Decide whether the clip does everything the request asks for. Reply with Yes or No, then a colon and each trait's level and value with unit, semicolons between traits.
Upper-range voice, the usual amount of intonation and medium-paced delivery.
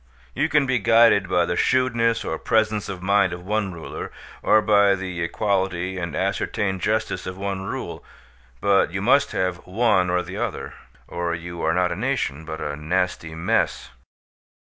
No: very low, 95 Hz; average, 3.5 semitones; average, 170 wpm